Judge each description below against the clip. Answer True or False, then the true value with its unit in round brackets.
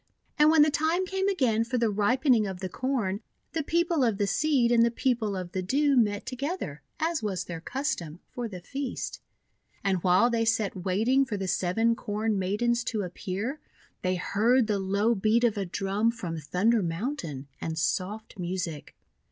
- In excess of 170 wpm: True (185 wpm)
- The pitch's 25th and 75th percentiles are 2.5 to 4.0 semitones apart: False (5.3 semitones)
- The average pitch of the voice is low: False (220 Hz)